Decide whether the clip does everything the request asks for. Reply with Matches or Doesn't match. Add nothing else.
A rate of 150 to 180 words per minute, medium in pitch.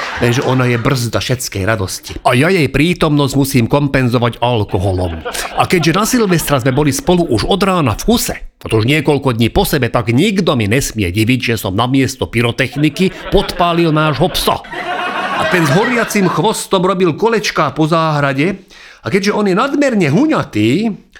Matches